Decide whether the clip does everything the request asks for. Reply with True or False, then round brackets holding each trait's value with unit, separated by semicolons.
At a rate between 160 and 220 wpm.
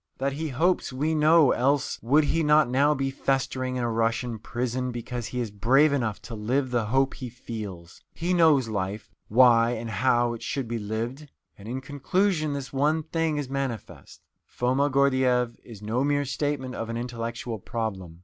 True (180 wpm)